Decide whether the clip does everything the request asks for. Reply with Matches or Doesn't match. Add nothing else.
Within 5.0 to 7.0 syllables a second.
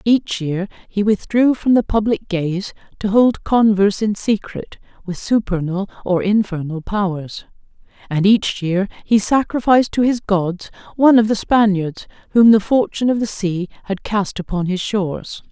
Doesn't match